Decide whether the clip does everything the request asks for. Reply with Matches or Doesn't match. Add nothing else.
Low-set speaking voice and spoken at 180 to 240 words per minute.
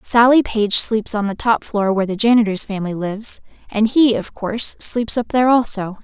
Doesn't match